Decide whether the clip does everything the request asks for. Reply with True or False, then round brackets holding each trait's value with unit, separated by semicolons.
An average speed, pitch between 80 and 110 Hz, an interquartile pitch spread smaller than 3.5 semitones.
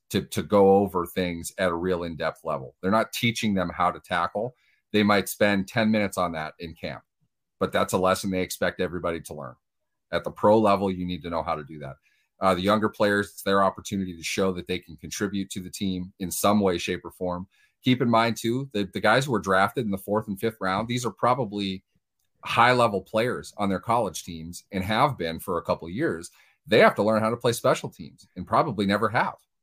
False (235 wpm; 100 Hz; 3.0 semitones)